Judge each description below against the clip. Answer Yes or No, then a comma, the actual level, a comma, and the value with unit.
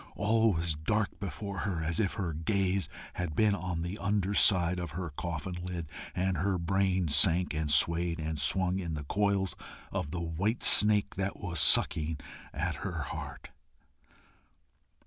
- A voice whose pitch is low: Yes, very low, 90 Hz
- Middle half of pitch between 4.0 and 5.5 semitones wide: No, average, 3.3 semitones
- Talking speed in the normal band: Yes, average, 155 wpm